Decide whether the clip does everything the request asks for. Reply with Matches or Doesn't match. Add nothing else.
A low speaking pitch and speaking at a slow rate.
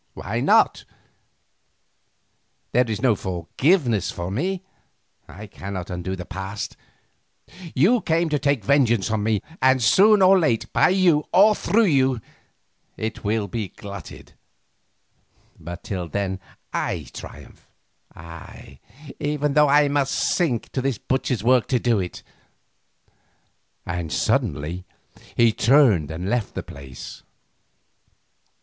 Matches